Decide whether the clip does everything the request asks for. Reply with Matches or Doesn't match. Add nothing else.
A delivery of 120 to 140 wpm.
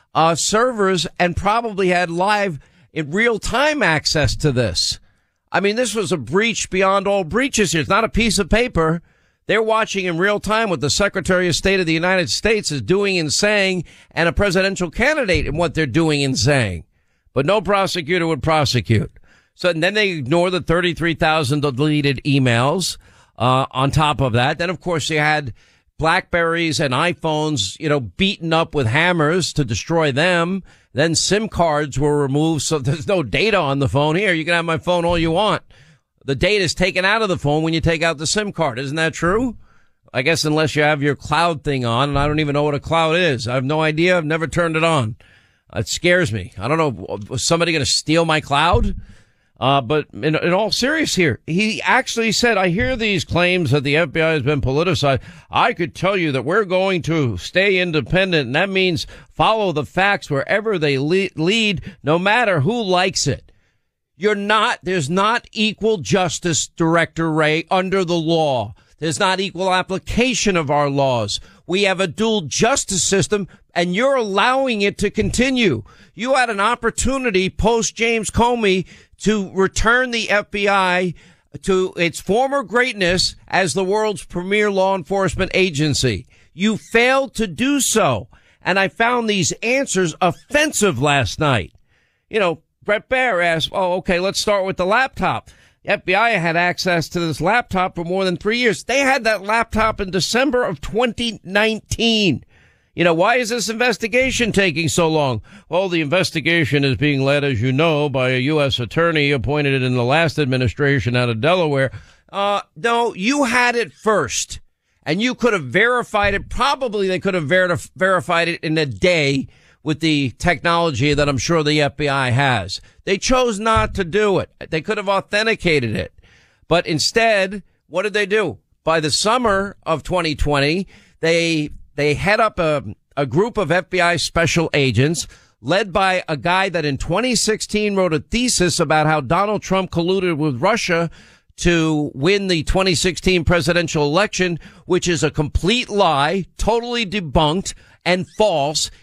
Doesn't match